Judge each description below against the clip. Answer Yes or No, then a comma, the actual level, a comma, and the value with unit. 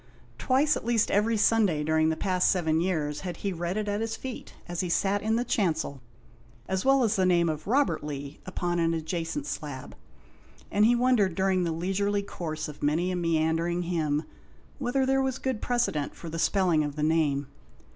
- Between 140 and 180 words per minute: No, average, 195 wpm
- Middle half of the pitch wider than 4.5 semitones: Yes, average, 5.2 semitones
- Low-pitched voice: No, medium, 180 Hz